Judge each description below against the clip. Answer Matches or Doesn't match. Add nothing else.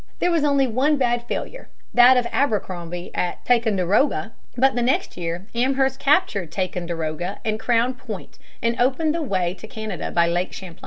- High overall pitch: Matches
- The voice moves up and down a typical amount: Doesn't match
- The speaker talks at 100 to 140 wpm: Doesn't match